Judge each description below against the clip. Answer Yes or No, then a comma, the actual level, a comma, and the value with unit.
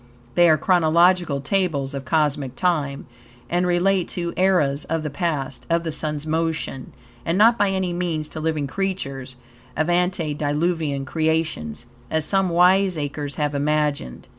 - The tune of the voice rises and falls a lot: No, average, 3.6 semitones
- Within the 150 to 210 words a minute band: No, average, 140 wpm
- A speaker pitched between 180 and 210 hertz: No, medium, 160 Hz